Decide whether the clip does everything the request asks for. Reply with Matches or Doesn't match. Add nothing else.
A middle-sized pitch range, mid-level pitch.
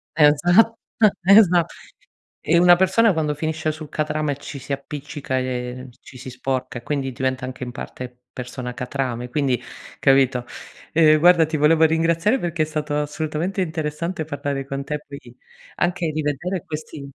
Matches